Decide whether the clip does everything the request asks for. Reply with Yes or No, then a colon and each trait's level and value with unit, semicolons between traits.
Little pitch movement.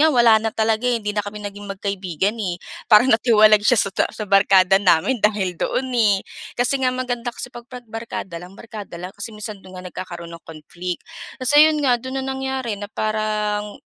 No: average, 3.8 semitones